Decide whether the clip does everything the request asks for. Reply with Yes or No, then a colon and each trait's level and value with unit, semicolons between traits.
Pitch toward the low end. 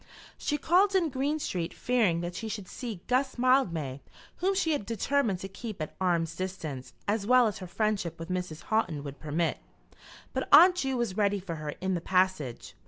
No: high, 195 Hz